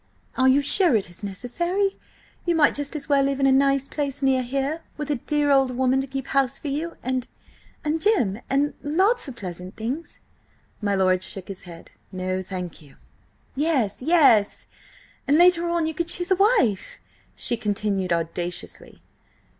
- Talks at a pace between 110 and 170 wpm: Yes, average, 160 wpm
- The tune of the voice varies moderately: No, wide, 7.0 semitones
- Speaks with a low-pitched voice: No, very high, 270 Hz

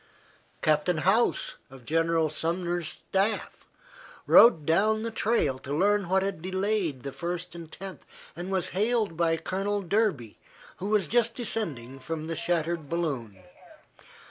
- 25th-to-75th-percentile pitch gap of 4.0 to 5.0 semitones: Yes, average, 4.4 semitones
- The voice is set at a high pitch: No, medium, 175 Hz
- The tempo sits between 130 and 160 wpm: Yes, average, 140 wpm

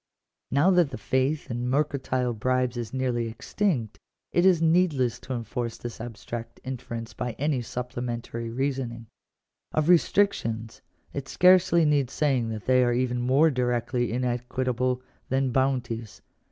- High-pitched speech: No, low, 125 Hz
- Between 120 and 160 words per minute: Yes, average, 140 wpm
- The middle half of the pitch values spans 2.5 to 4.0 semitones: Yes, average, 2.8 semitones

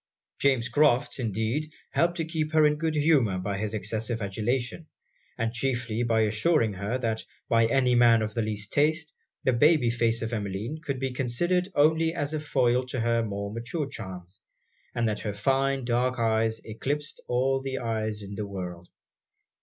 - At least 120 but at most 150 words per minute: No, average, 175 wpm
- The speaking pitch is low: Yes, low, 120 Hz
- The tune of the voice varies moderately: Yes, average, 4.2 semitones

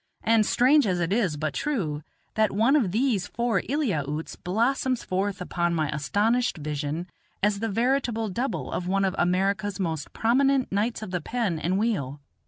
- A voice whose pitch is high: Yes, high, 200 Hz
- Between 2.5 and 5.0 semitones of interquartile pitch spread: No, wide, 5.4 semitones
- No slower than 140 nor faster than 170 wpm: Yes, average, 165 wpm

